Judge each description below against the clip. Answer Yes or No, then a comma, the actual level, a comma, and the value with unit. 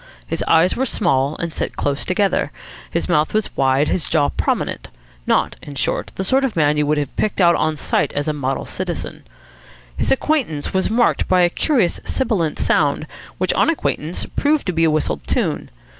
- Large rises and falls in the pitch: Yes, wide, 6.0 semitones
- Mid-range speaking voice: Yes, medium, 165 Hz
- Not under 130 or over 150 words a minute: No, average, 190 wpm